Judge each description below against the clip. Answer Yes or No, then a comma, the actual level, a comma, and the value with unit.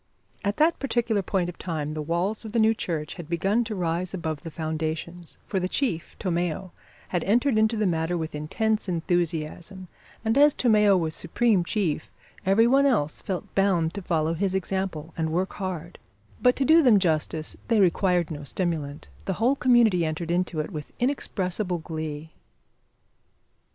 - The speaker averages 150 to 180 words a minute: Yes, average, 170 wpm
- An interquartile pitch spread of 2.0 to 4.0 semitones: No, average, 4.7 semitones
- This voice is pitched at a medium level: Yes, medium, 180 Hz